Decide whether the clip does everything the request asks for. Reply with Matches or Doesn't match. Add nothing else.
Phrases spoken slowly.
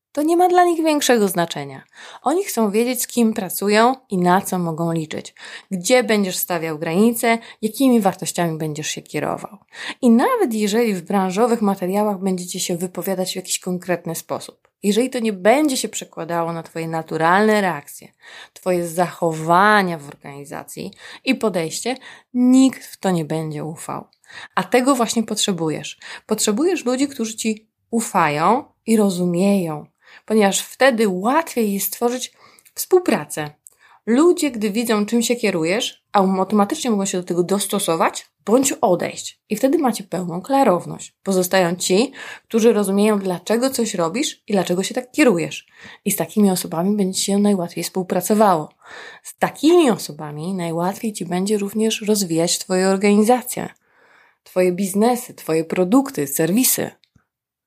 Doesn't match